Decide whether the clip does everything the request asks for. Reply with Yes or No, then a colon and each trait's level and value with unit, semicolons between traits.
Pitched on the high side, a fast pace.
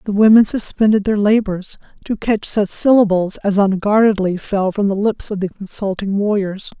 No: high, 205 Hz; average, 170 wpm